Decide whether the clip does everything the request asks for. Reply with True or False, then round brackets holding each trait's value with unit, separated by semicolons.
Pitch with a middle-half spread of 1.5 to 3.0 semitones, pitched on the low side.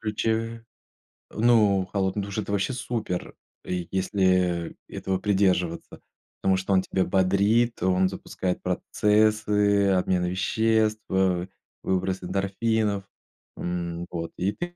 True (2.6 semitones; 95 Hz)